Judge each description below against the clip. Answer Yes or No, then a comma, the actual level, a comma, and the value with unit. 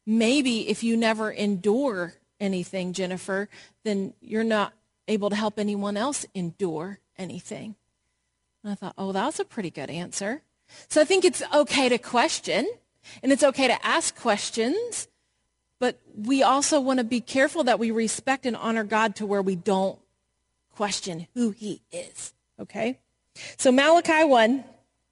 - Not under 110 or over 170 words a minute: Yes, average, 155 wpm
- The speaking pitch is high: Yes, high, 215 Hz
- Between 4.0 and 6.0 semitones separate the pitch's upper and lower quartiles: Yes, average, 5.2 semitones